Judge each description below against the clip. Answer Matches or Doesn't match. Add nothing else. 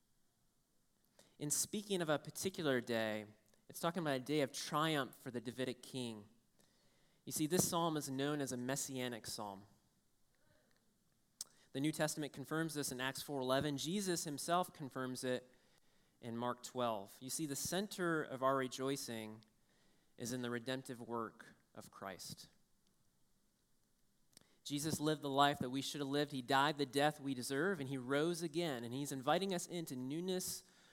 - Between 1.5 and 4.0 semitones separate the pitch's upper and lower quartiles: Matches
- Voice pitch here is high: Doesn't match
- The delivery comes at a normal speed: Matches